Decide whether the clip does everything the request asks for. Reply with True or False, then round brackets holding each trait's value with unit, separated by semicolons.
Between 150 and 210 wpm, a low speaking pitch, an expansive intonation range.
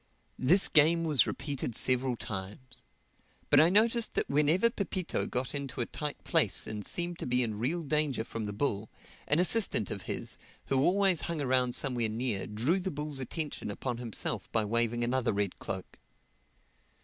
True (170 wpm; 130 Hz; 5.7 semitones)